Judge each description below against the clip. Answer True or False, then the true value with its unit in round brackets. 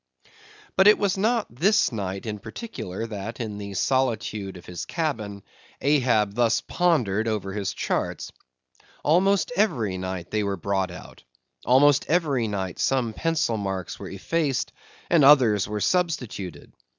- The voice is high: False (115 Hz)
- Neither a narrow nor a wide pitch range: False (7.4 semitones)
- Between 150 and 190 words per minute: False (140 wpm)